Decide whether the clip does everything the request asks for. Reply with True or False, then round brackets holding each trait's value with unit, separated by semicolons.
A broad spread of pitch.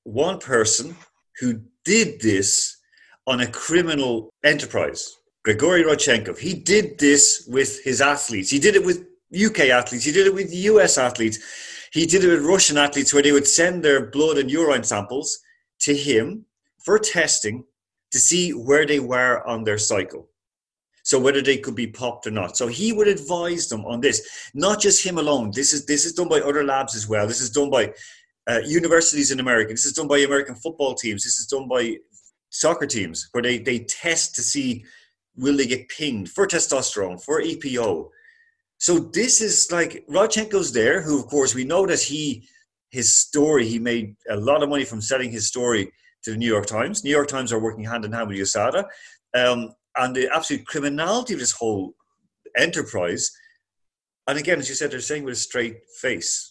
True (7.2 semitones)